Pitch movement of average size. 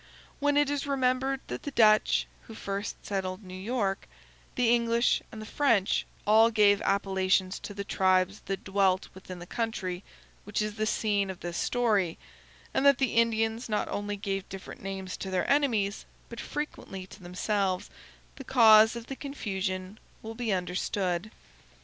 Yes: average, 3.4 semitones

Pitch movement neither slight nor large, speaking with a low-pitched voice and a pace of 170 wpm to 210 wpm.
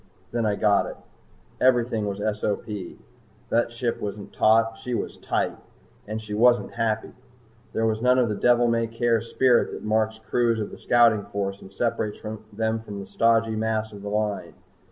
No: narrow, 1.9 semitones; low, 110 Hz; average, 175 wpm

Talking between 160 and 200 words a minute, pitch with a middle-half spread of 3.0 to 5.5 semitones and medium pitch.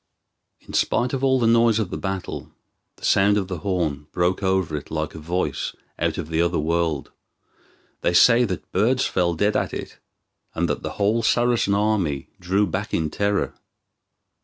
No: average, 180 wpm; average, 4.3 semitones; very low, 95 Hz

